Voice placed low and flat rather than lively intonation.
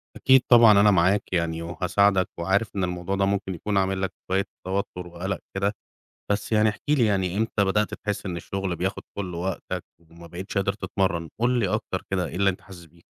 Yes: very low, 95 Hz; narrow, 2.2 semitones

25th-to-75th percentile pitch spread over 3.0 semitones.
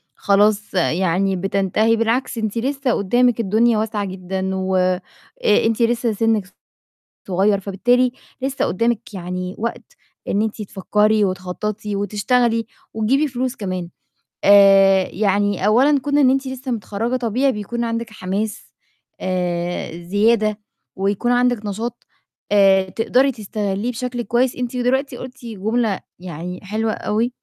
Yes: average, 3.7 semitones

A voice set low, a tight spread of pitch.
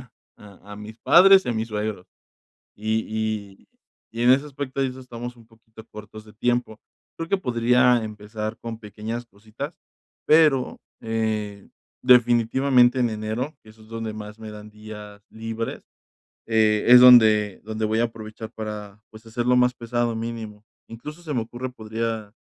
Yes: low, 110 Hz; narrow, 2.3 semitones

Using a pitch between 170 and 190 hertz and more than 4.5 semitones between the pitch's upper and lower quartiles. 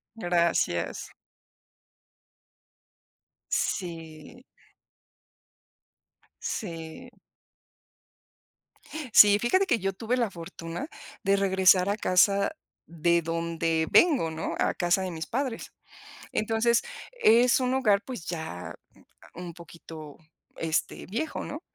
Yes: medium, 185 Hz; wide, 5.6 semitones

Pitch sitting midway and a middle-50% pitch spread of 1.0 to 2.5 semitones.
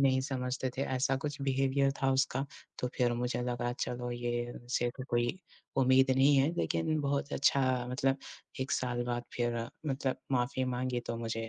No: low, 130 Hz; narrow, 1.9 semitones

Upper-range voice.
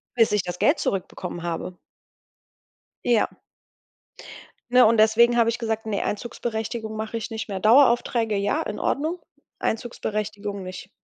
Yes: high, 220 Hz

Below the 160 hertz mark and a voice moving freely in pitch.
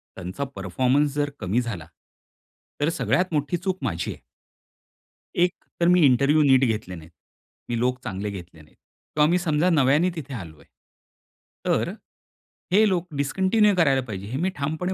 Yes: medium, 140 Hz; wide, 8.5 semitones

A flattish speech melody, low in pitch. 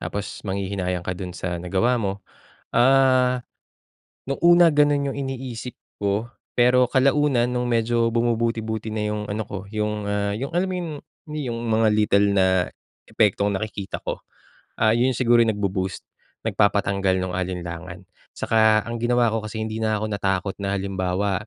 No: average, 3.8 semitones; low, 110 Hz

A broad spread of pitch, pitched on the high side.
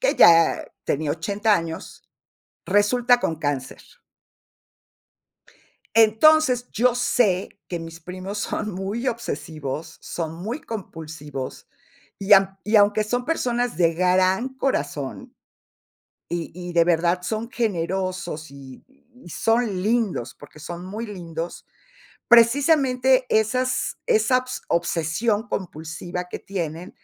Yes: wide, 6.1 semitones; high, 195 Hz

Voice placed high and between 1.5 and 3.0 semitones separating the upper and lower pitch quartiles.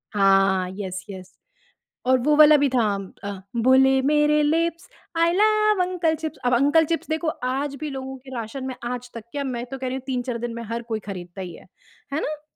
No: very high, 265 Hz; average, 4.6 semitones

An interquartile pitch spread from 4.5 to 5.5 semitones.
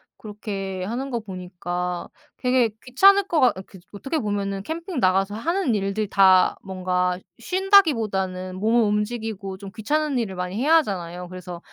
Yes: average, 5.2 semitones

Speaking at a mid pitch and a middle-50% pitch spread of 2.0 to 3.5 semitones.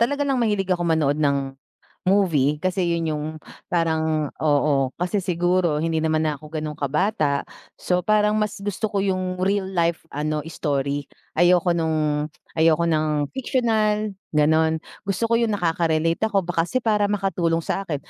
No: medium, 170 Hz; average, 4.3 semitones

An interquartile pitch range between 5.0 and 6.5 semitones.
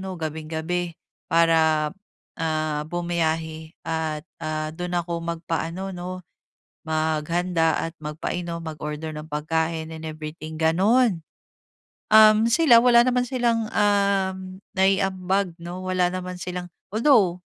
No: average, 3.0 semitones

